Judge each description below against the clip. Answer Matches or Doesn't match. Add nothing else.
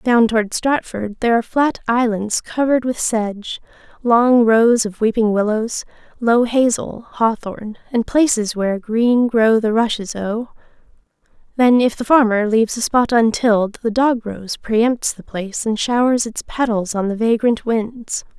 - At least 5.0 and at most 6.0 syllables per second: Doesn't match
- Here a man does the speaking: Doesn't match